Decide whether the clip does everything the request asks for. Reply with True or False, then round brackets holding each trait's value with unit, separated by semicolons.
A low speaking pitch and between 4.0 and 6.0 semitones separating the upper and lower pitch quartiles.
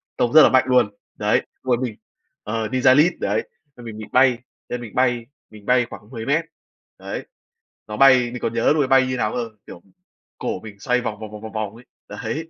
False (120 Hz; 3.0 semitones)